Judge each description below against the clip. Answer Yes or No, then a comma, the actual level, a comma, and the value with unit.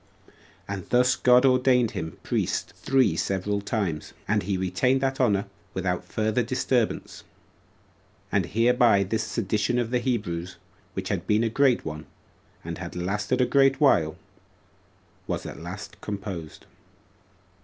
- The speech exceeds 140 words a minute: No, slow, 135 wpm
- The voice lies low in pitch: Yes, low, 110 Hz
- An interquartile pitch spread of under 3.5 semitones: No, average, 4.9 semitones